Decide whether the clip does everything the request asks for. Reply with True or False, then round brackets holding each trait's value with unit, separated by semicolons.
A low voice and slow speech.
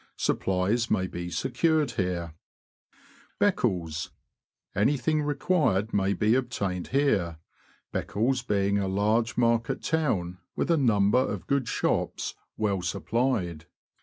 True (110 Hz; 115 wpm)